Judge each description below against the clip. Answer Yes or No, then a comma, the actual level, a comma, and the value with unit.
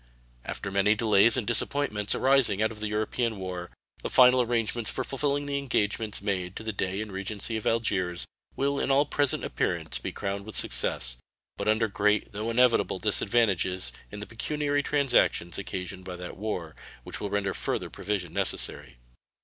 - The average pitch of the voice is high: No, low, 105 Hz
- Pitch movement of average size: Yes, average, 3.8 semitones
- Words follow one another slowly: No, average, 170 wpm